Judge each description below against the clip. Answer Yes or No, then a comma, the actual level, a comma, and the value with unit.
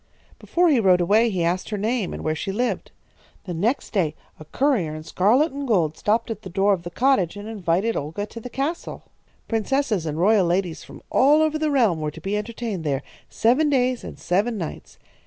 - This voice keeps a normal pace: No, fast, 210 wpm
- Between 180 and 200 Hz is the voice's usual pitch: No, high, 210 Hz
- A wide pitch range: Yes, wide, 6.1 semitones